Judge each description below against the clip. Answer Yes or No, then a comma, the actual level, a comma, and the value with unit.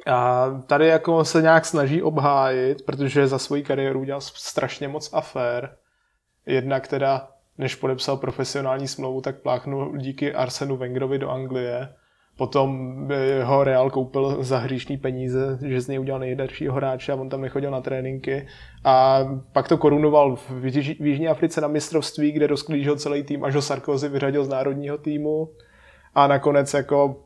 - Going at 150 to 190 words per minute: Yes, average, 155 wpm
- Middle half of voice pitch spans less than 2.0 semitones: Yes, narrow, 1.6 semitones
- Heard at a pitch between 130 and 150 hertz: Yes, low, 135 Hz